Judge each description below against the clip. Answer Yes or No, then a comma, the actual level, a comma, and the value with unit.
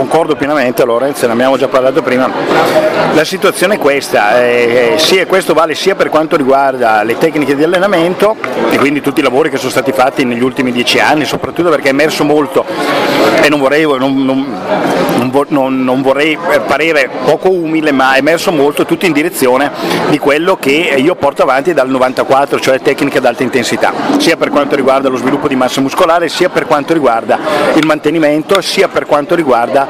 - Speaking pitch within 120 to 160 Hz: Yes, medium, 140 Hz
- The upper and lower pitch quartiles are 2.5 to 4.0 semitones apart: Yes, average, 2.8 semitones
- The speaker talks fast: Yes, fast, 190 wpm